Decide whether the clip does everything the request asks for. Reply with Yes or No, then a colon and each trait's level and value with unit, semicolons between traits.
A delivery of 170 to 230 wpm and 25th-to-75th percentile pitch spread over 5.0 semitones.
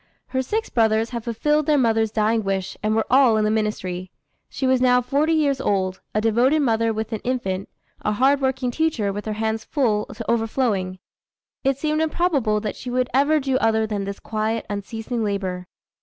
No: average, 190 wpm; average, 3.8 semitones